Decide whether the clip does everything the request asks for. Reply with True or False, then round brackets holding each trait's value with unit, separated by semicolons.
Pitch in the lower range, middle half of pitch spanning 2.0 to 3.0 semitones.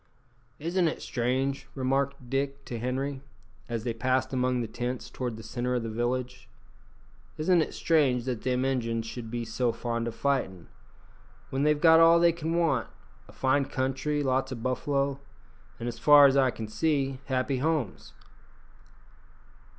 True (130 Hz; 2.7 semitones)